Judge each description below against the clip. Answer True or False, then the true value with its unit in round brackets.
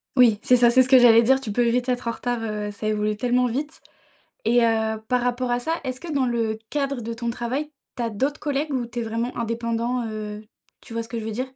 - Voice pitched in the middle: False (240 Hz)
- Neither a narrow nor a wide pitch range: False (2.0 semitones)